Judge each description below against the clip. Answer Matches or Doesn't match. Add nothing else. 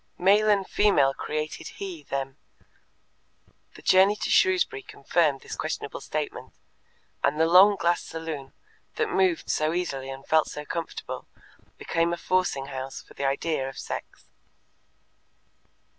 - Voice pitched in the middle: Matches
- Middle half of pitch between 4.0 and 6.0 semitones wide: Matches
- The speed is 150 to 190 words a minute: Doesn't match